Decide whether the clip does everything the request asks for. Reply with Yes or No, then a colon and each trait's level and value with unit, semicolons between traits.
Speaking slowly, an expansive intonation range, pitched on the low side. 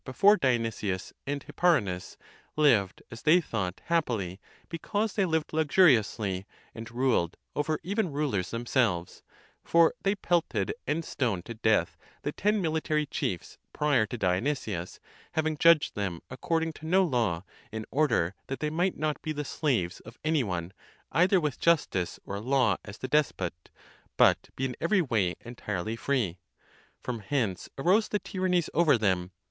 No: average, 150 wpm; wide, 7.8 semitones; low, 130 Hz